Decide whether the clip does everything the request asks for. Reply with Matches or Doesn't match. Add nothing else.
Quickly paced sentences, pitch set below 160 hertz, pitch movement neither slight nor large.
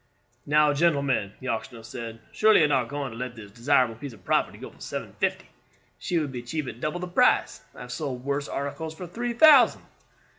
Matches